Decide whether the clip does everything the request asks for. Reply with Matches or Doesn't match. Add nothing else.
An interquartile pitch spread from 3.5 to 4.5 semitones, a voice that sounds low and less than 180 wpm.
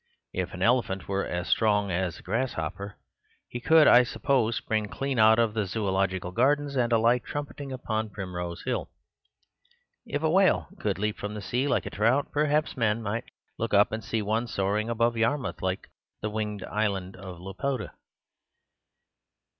Matches